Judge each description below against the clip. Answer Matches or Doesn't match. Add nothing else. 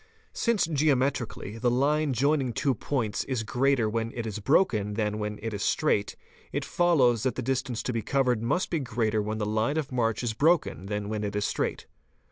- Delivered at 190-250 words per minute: Matches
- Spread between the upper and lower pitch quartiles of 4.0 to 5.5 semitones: Matches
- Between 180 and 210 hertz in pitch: Doesn't match